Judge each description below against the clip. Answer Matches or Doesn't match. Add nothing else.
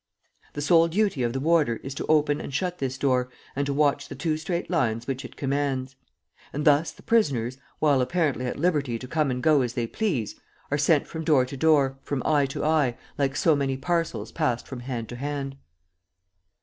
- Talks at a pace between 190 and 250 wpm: Matches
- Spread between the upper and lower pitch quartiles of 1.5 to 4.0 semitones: Matches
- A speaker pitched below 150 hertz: Matches